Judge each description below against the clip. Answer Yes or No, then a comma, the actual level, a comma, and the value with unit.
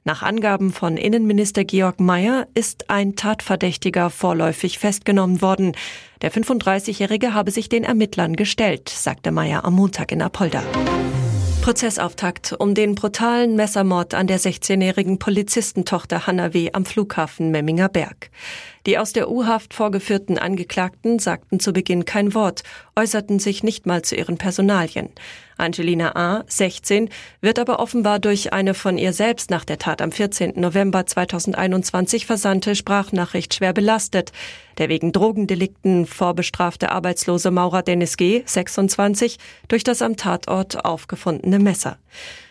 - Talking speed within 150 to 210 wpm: No, average, 135 wpm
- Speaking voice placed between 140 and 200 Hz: Yes, high, 190 Hz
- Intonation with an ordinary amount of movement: Yes, average, 3.0 semitones